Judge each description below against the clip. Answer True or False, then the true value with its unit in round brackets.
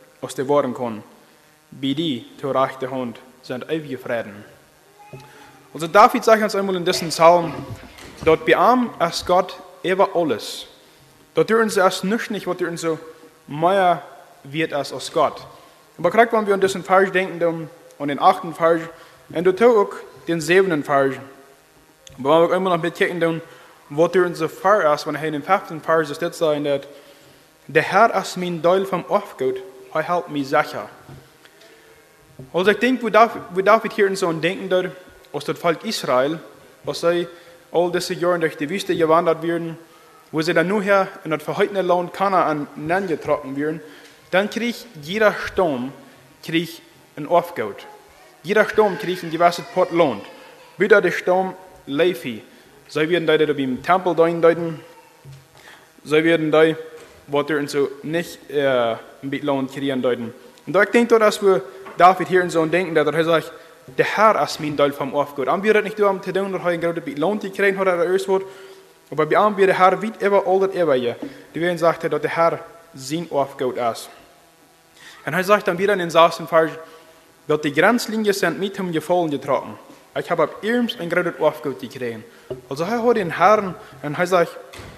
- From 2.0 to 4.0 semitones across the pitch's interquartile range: True (3.7 semitones)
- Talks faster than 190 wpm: False (175 wpm)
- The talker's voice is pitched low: False (165 Hz)